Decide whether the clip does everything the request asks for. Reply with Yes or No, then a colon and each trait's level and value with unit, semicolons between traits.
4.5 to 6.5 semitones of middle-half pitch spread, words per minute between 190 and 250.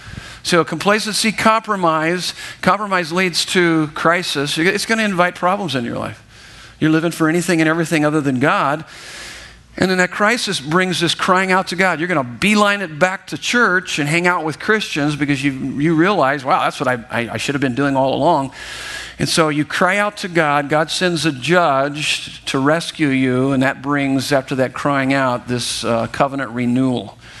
Yes: average, 5.0 semitones; average, 195 wpm